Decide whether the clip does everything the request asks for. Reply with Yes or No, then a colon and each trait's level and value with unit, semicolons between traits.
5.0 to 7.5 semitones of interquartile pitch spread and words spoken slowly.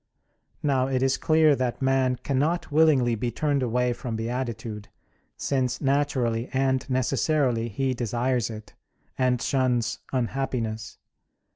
No: narrow, 2.4 semitones; slow, 120 wpm